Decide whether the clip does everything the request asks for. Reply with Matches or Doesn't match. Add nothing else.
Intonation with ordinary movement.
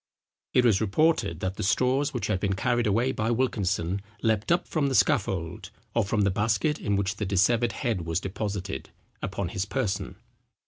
Matches